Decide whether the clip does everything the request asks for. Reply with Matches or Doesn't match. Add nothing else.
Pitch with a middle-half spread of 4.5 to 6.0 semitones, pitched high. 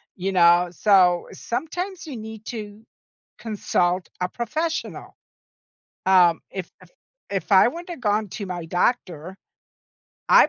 Matches